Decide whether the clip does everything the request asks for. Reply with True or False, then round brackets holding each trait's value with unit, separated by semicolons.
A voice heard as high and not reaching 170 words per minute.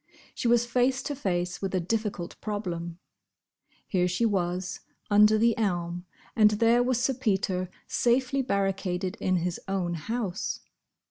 True (200 Hz; 140 wpm)